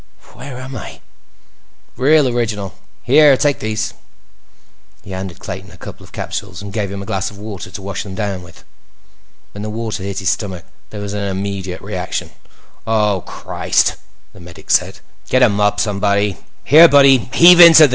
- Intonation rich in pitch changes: No, average, 3.9 semitones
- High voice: No, low, 105 Hz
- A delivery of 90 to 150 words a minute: No, average, 175 wpm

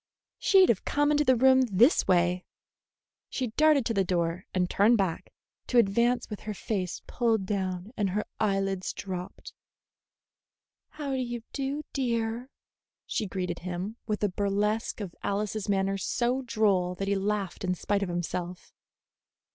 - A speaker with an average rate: Yes, average, 155 wpm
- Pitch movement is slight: No, average, 4.3 semitones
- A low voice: No, high, 205 Hz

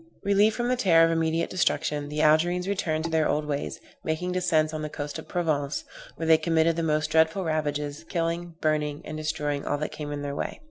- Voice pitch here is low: No, medium, 160 Hz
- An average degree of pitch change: No, narrow, 1.9 semitones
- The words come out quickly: Yes, fast, 215 wpm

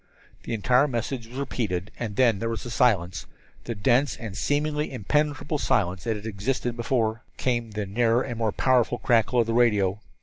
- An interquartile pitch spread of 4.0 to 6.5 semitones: No, average, 3.2 semitones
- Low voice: Yes, low, 115 Hz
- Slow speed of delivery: No, average, 175 wpm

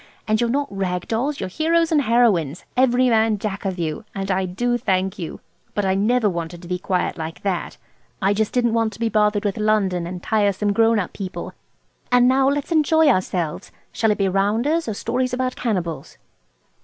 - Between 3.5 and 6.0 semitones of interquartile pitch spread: Yes, average, 4.6 semitones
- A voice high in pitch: Yes, high, 210 Hz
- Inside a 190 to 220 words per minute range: Yes, average, 195 wpm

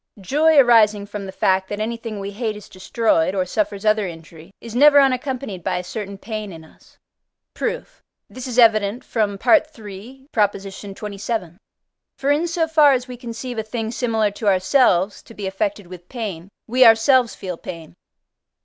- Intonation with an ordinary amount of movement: Yes, average, 3.9 semitones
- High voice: Yes, high, 215 Hz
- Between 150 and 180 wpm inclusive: Yes, average, 165 wpm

